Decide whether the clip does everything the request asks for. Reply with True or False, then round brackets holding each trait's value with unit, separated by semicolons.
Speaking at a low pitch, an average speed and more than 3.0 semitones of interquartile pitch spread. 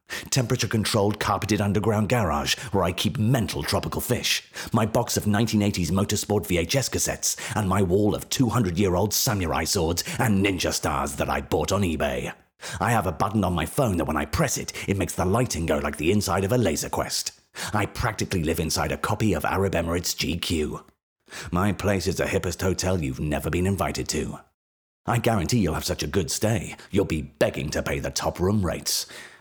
True (95 Hz; 190 wpm; 4.4 semitones)